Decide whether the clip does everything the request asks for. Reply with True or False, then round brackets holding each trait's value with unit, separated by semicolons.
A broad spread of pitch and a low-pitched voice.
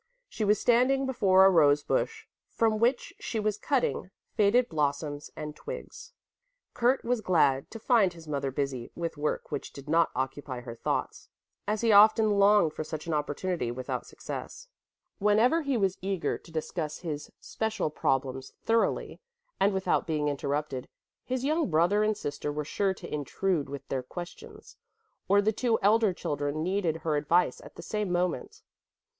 False (6.6 semitones; 180 Hz)